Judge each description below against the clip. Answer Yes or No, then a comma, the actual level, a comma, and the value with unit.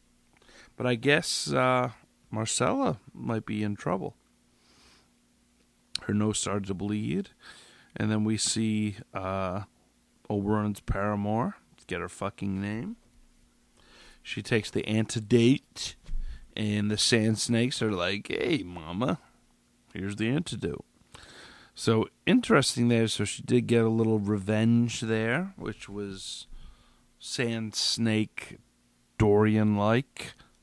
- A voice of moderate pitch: No, low, 105 Hz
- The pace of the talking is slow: Yes, slow, 110 wpm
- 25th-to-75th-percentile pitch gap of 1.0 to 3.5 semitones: Yes, average, 3.1 semitones